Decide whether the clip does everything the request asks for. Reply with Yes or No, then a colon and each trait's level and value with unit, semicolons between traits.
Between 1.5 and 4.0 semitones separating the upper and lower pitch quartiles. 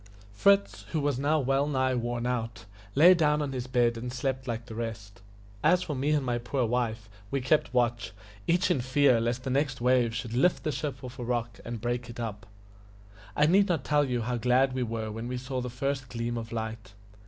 Yes: average, 2.9 semitones